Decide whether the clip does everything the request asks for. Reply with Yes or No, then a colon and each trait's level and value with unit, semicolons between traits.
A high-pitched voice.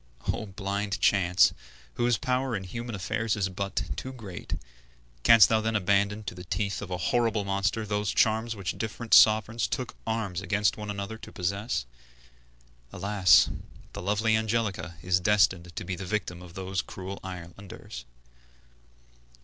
No: low, 100 Hz